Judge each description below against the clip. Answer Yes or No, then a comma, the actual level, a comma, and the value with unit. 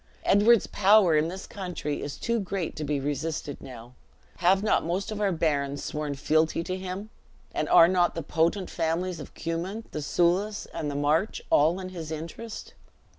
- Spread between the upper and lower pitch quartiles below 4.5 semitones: Yes, average, 4.0 semitones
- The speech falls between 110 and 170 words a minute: No, average, 180 wpm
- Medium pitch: Yes, medium, 170 Hz